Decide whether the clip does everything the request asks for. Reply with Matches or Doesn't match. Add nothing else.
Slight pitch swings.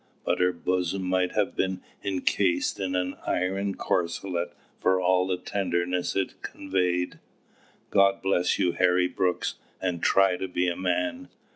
Matches